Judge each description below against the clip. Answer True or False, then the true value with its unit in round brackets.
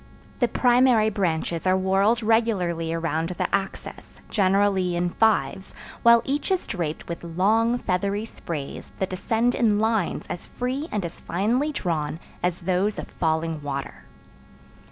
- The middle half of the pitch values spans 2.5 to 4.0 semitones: False (4.8 semitones)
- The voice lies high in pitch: True (195 Hz)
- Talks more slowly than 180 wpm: True (140 wpm)